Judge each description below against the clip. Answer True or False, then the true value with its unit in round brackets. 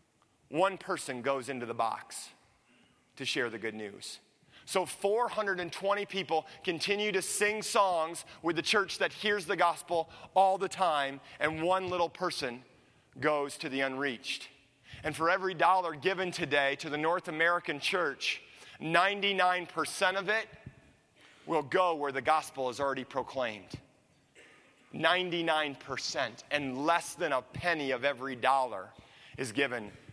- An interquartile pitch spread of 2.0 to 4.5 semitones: False (5.1 semitones)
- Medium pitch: True (160 Hz)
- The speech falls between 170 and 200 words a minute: False (135 wpm)